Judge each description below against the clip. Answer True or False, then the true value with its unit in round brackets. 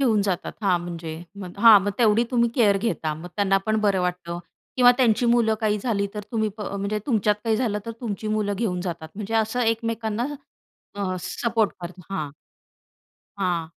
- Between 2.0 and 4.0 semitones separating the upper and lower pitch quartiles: True (3.4 semitones)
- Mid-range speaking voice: False (210 Hz)